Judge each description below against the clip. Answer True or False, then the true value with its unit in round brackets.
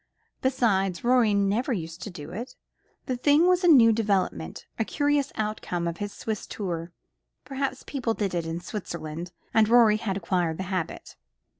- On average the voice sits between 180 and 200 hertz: False (210 Hz)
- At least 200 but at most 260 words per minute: False (165 wpm)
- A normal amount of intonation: False (5.7 semitones)